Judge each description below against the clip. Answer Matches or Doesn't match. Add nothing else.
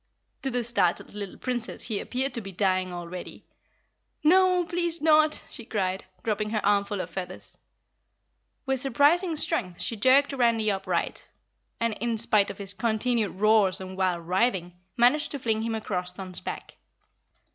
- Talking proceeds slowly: Doesn't match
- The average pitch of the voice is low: Doesn't match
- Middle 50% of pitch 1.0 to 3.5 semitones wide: Doesn't match